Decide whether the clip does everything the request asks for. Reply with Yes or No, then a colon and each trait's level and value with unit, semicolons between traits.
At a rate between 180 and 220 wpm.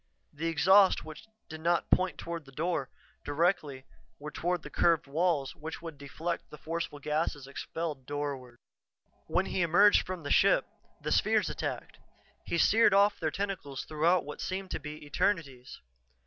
No: average, 160 wpm